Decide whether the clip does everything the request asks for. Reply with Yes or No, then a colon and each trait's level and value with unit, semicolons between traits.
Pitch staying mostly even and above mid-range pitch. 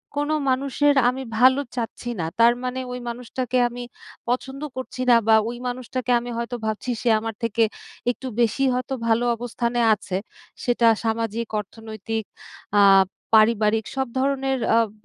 Yes: narrow, 2.3 semitones; high, 240 Hz